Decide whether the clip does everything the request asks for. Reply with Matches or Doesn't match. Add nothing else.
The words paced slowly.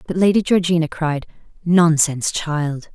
Matches